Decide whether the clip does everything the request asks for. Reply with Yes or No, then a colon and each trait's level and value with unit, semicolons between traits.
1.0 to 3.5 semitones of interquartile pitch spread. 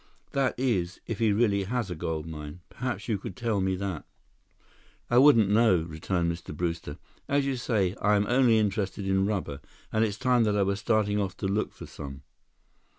No: average, 4.2 semitones